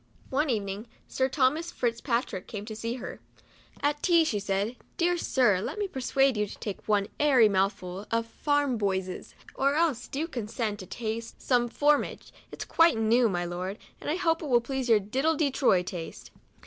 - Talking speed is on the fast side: Yes, fast, 210 wpm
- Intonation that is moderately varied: No, wide, 5.8 semitones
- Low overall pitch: No, high, 235 Hz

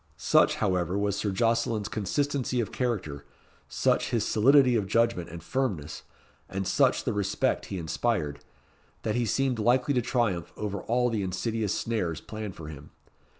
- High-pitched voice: No, low, 105 Hz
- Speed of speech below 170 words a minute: Yes, average, 155 wpm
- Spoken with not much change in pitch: No, average, 4.4 semitones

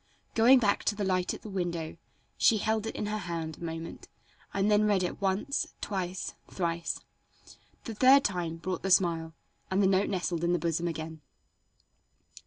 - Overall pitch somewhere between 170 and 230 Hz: Yes, medium, 185 Hz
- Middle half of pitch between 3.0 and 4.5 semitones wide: Yes, average, 3.5 semitones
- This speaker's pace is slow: No, average, 180 wpm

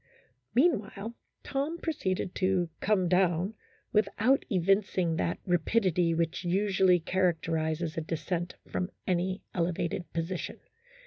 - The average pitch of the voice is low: No, medium, 185 Hz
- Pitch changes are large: No, average, 2.8 semitones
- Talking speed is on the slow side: Yes, slow, 110 wpm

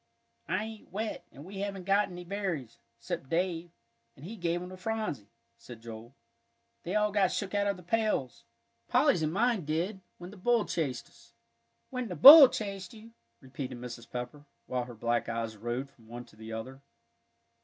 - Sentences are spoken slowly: No, average, 185 wpm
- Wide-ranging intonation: Yes, wide, 8.4 semitones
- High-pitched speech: No, medium, 175 Hz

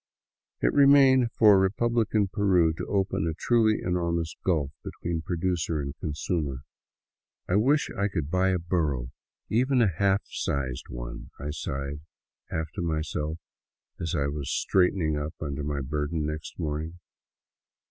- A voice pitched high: No, very low, 85 Hz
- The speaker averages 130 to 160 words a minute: Yes, average, 145 wpm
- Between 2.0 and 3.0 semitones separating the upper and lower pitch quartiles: No, average, 4.8 semitones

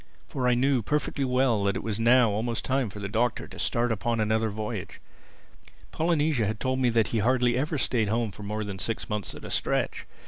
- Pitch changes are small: No, average, 3.2 semitones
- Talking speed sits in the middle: No, fast, 220 wpm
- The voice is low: Yes, low, 115 Hz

